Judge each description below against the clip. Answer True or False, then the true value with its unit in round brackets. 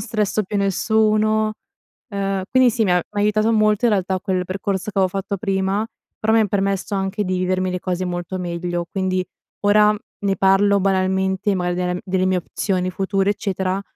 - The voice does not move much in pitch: True (2.1 semitones)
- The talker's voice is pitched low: False (195 Hz)